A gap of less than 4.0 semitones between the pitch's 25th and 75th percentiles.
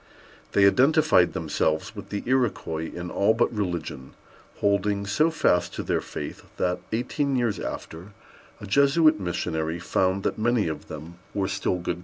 No: wide, 5.6 semitones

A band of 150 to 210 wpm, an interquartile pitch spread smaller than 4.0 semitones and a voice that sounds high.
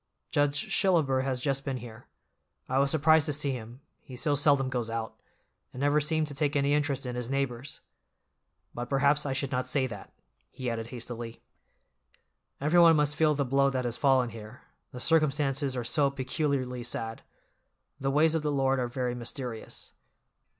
No: average, 175 wpm; average, 2.9 semitones; low, 135 Hz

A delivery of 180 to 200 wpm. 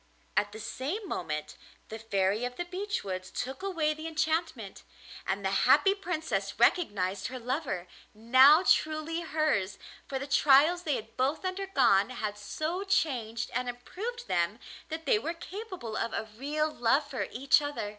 No: average, 160 wpm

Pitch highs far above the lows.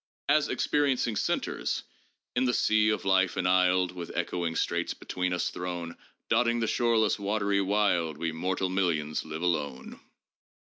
No: average, 3.7 semitones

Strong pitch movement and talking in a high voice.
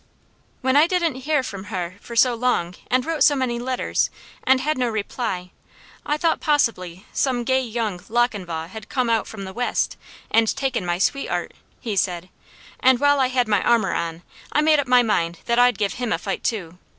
No: average, 5.0 semitones; high, 240 Hz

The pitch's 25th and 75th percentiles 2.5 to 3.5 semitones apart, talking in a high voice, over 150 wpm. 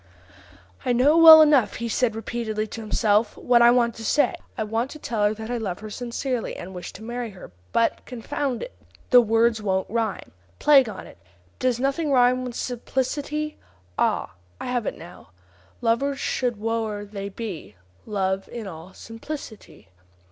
Yes: average, 3.0 semitones; high, 230 Hz; average, 170 wpm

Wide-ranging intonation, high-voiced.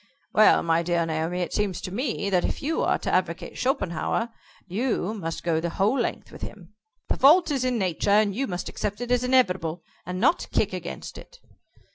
Yes: wide, 6.2 semitones; high, 195 Hz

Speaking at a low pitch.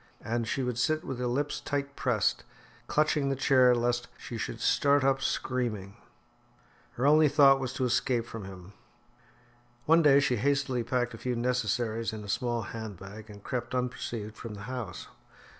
Yes: low, 125 Hz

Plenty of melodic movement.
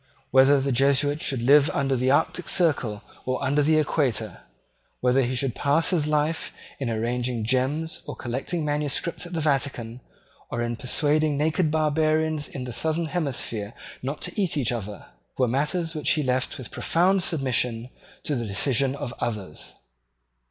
No: average, 3.8 semitones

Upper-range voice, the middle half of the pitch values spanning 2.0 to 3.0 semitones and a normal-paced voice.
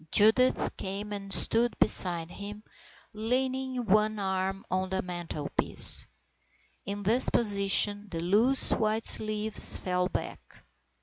No: high, 205 Hz; narrow, 2.6 semitones; slow, 115 wpm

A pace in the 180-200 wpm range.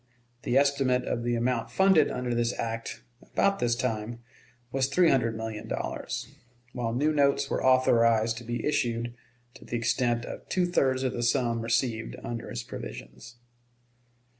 No: average, 160 wpm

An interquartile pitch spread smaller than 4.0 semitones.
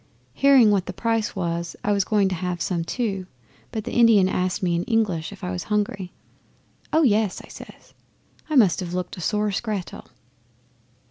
Yes: average, 3.6 semitones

